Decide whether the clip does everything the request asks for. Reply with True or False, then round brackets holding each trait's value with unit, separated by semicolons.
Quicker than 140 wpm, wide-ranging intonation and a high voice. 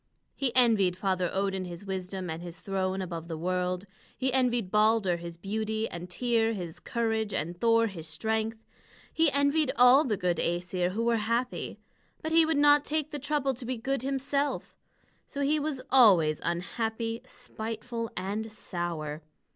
True (165 wpm; 5.8 semitones; 220 Hz)